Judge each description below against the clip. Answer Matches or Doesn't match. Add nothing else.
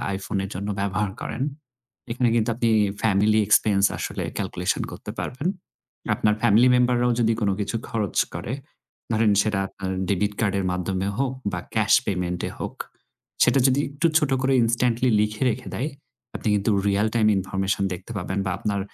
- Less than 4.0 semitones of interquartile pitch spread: Matches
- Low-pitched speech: Matches